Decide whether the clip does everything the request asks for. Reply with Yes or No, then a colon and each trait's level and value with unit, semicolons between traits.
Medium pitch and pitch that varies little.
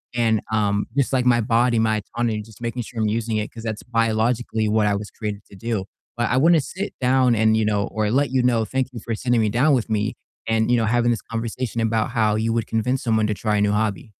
No: low, 115 Hz; narrow, 2.0 semitones